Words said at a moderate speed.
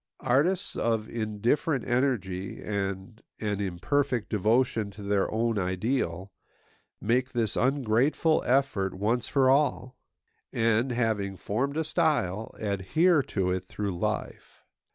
No: slow, 115 wpm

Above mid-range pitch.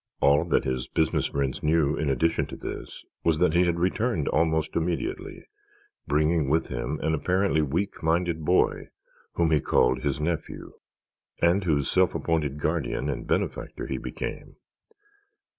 No: very low, 80 Hz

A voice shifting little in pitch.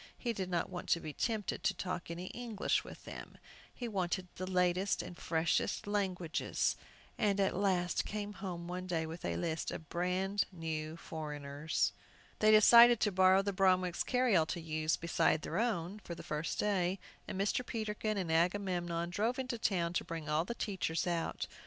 No: average, 3.4 semitones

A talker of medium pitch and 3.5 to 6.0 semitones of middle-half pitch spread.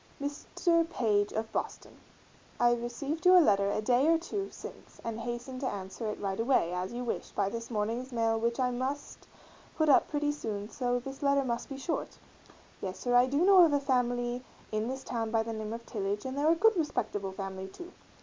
No: high, 245 Hz; average, 4.5 semitones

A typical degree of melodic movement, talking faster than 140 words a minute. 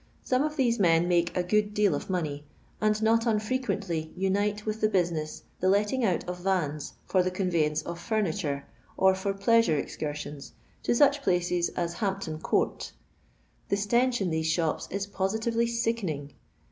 Yes: average, 4.2 semitones; average, 160 wpm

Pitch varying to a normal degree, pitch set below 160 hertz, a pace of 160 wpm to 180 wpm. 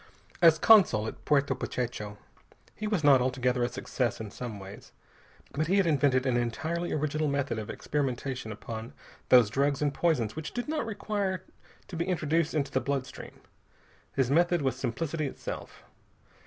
Yes: average, 5.0 semitones; medium, 140 Hz; average, 165 wpm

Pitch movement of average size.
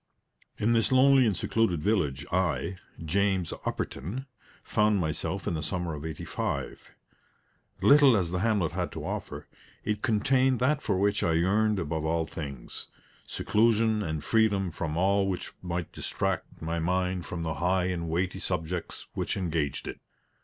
Yes: average, 4.4 semitones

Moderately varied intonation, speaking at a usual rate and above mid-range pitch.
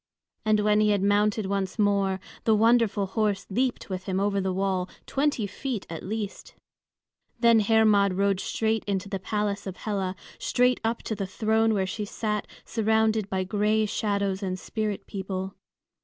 No: narrow, 2.1 semitones; average, 165 wpm; high, 205 Hz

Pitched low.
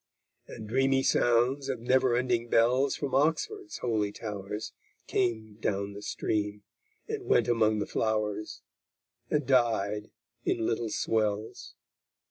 Yes: low, 115 Hz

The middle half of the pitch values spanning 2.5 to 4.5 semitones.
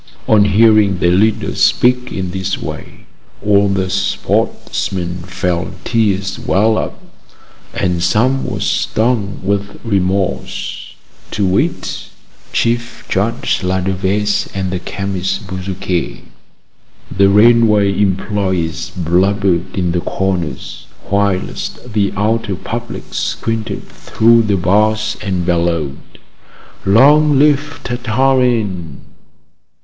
Yes: average, 2.9 semitones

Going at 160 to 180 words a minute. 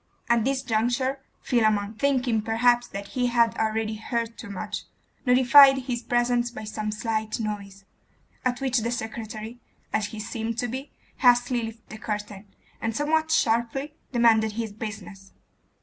No: average, 150 wpm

